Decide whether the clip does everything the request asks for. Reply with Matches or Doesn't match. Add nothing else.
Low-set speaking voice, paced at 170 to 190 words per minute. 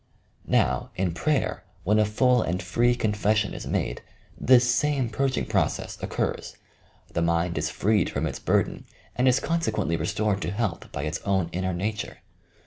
Doesn't match